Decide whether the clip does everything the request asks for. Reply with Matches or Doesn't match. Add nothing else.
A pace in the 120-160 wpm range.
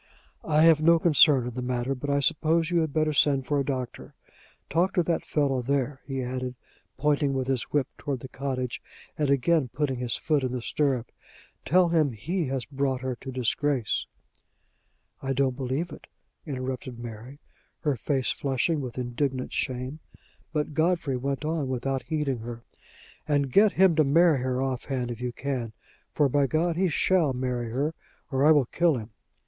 Doesn't match